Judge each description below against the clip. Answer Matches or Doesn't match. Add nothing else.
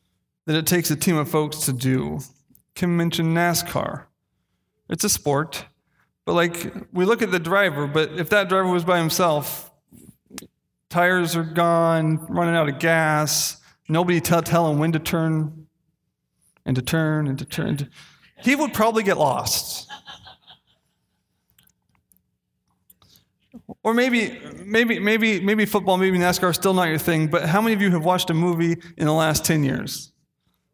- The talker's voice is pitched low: Doesn't match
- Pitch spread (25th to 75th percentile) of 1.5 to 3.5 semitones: Matches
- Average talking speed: Matches